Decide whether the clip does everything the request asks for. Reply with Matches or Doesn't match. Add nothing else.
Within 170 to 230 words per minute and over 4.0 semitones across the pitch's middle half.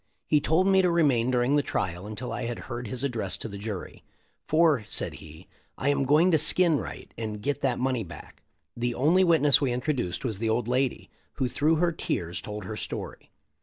Matches